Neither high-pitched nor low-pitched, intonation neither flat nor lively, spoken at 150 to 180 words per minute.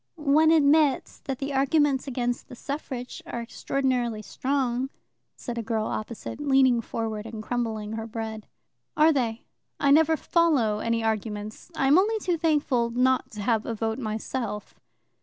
No: high, 245 Hz; average, 4.1 semitones; average, 155 wpm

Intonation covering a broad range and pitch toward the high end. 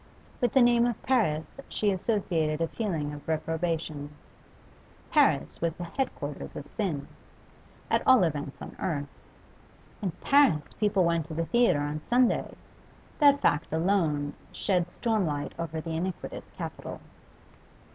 No: wide, 5.7 semitones; medium, 170 Hz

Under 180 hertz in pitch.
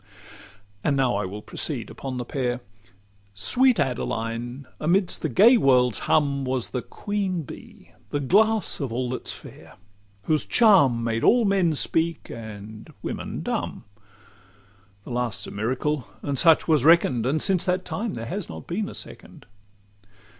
Yes: medium, 140 Hz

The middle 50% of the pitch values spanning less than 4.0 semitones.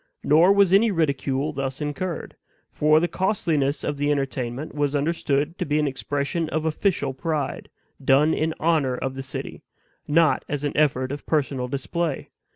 Yes: average, 2.8 semitones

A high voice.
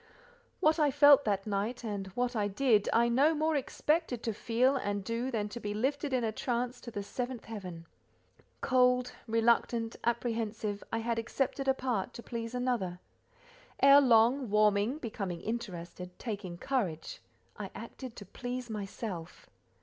Yes: high, 235 Hz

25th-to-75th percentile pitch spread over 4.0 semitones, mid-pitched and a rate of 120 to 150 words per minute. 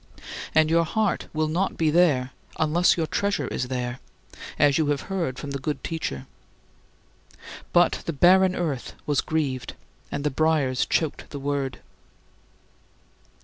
No: average, 3.5 semitones; medium, 155 Hz; average, 145 wpm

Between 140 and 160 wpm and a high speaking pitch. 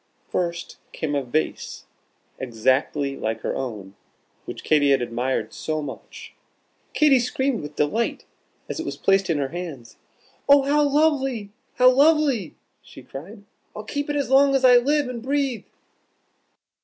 Yes: average, 150 wpm; high, 200 Hz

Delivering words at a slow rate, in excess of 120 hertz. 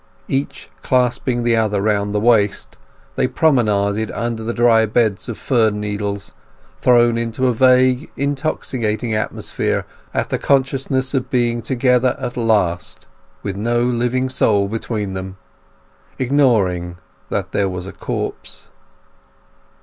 No: slow, 125 wpm; low, 115 Hz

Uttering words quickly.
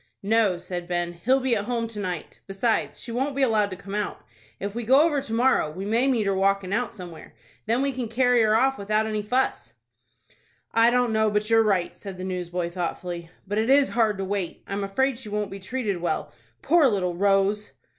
Yes: fast, 215 wpm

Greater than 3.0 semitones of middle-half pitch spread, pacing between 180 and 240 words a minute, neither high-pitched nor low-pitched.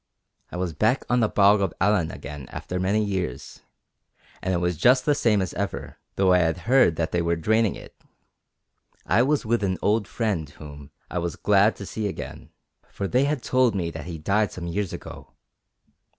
No: average, 4.3 semitones; average, 195 wpm; very low, 95 Hz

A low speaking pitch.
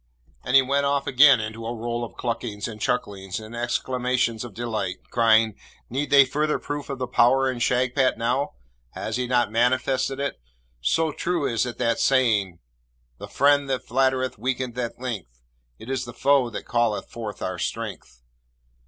Yes: low, 125 Hz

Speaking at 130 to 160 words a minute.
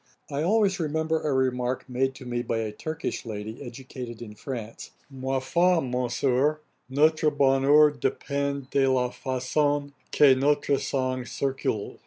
Yes: average, 140 wpm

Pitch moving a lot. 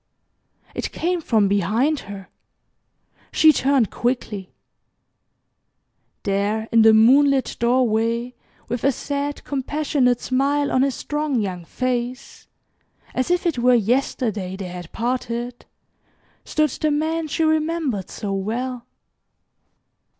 No: average, 4.6 semitones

